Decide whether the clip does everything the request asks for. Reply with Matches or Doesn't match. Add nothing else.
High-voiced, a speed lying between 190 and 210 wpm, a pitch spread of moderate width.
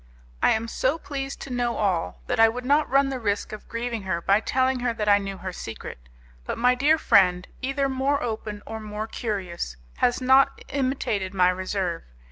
Matches